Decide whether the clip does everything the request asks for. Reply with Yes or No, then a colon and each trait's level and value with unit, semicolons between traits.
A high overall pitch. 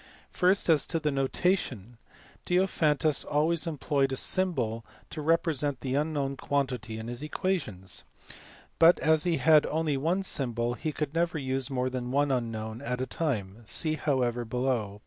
No: medium, 140 Hz